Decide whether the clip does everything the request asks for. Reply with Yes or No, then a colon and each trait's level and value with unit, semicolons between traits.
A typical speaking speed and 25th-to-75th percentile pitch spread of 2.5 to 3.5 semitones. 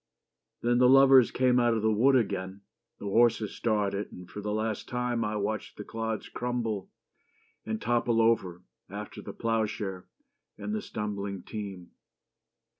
Yes: average, 150 wpm; average, 3.0 semitones